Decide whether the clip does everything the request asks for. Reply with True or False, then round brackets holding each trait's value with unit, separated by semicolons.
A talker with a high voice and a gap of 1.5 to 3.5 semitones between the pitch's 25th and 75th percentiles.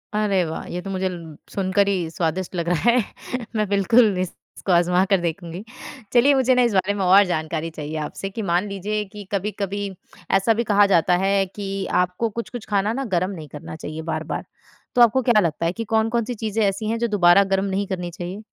True (195 Hz; 3.2 semitones)